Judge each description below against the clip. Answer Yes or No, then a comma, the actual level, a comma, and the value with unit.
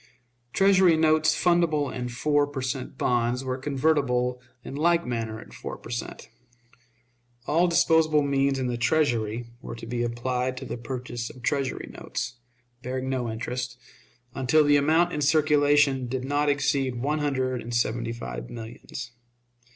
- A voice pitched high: No, low, 130 Hz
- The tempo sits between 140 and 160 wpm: Yes, average, 150 wpm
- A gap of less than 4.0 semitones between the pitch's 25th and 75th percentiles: Yes, average, 3.3 semitones